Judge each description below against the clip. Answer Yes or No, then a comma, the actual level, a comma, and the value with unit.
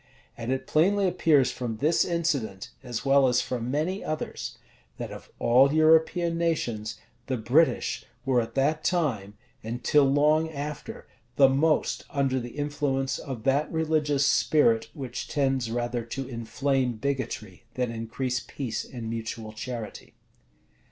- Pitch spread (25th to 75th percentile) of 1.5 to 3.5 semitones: No, average, 4.2 semitones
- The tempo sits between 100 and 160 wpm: Yes, average, 140 wpm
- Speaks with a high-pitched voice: No, low, 135 Hz